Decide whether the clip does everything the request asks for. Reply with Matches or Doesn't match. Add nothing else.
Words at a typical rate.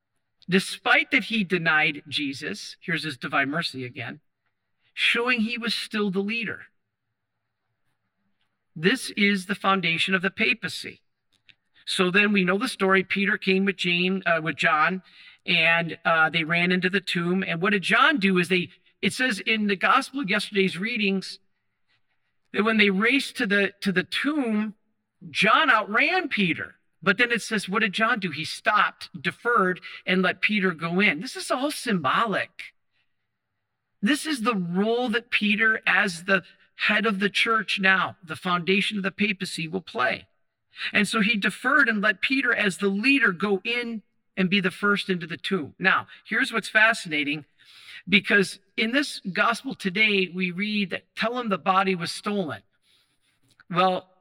Matches